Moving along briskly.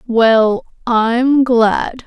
No: slow, 85 wpm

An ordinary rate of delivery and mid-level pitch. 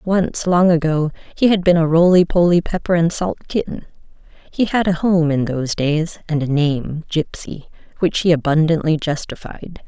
Yes: average, 170 wpm; medium, 165 Hz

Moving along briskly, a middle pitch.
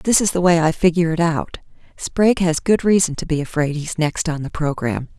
Yes: fast, 230 wpm; medium, 165 Hz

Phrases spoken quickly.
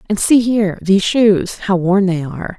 No: average, 165 wpm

